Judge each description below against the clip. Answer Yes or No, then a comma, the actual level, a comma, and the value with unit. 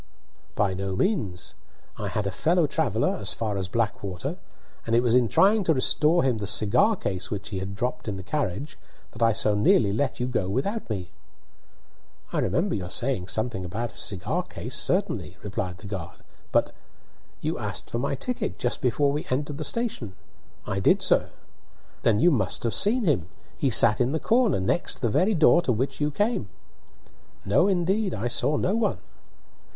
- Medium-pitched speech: No, low, 120 Hz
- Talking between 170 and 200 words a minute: Yes, average, 190 wpm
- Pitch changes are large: Yes, wide, 7.4 semitones